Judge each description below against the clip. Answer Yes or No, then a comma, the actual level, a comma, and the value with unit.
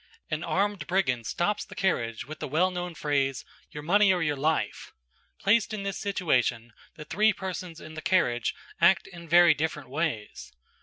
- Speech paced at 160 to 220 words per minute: Yes, average, 170 wpm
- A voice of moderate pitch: Yes, medium, 165 Hz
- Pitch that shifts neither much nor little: Yes, average, 4.8 semitones